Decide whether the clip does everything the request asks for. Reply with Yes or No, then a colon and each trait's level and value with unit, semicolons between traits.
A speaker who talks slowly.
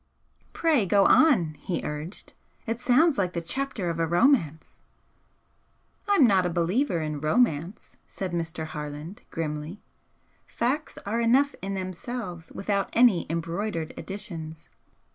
Yes: slow, 125 wpm